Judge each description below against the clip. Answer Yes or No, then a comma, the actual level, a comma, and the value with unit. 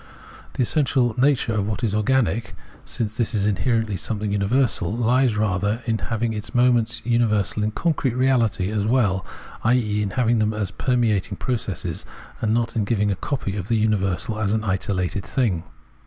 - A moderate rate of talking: Yes, average, 170 wpm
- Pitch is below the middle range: Yes, low, 110 Hz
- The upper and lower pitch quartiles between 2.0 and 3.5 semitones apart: Yes, average, 2.9 semitones